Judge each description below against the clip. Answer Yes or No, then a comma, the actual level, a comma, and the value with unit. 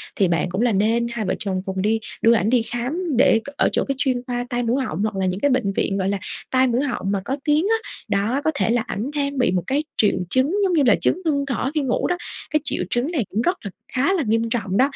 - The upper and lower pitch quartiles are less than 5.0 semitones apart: No, wide, 5.4 semitones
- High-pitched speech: Yes, high, 240 Hz